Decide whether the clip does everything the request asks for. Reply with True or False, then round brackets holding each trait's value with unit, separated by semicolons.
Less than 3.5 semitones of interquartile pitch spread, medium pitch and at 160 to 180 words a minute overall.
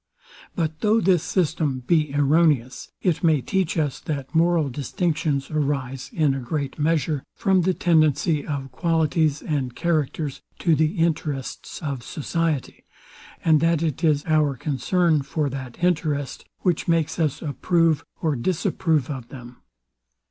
False (3.0 semitones; 155 Hz; 140 wpm)